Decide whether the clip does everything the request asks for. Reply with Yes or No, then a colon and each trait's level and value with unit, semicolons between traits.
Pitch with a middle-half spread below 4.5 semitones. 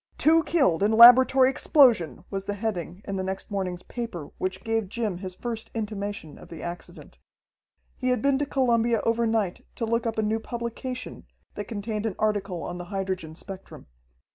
Yes: average, 3.7 semitones